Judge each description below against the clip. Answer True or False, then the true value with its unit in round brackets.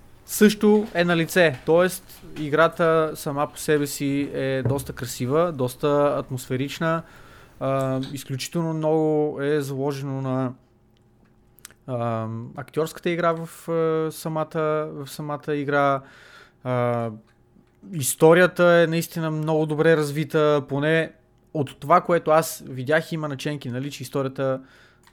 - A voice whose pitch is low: False (150 Hz)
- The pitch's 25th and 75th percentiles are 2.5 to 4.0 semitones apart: True (3.5 semitones)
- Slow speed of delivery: True (110 wpm)